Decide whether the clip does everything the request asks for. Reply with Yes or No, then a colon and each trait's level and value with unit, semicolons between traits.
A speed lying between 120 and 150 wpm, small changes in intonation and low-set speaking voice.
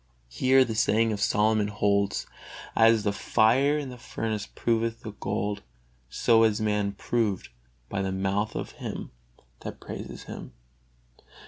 Yes: average, 140 wpm; narrow, 2.0 semitones; low, 110 Hz